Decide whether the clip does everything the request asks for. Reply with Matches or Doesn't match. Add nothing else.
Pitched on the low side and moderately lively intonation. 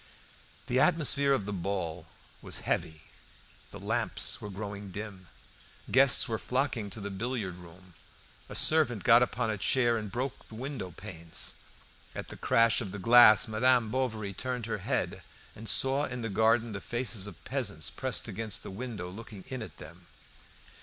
Matches